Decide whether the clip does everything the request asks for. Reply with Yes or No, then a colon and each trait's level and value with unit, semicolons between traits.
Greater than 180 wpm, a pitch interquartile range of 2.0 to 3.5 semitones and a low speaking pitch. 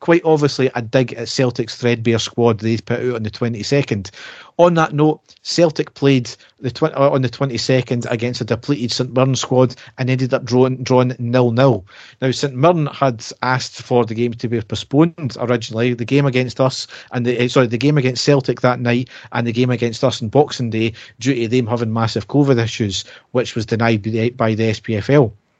Yes: average, 200 wpm; narrow, 2.5 semitones; low, 125 Hz